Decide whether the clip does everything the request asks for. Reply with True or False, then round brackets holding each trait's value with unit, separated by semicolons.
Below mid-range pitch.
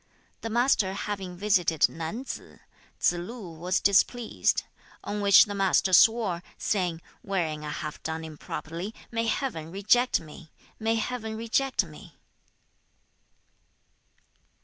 False (195 Hz)